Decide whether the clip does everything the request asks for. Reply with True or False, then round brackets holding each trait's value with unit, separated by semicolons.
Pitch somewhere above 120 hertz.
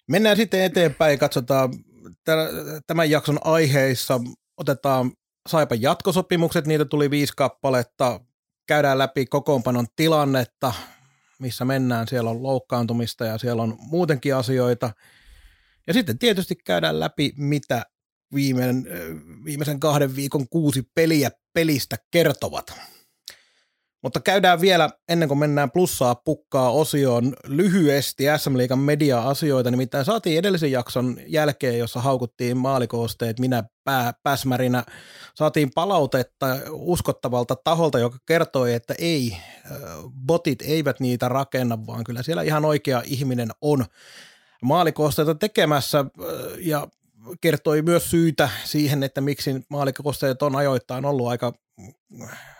True (140 Hz)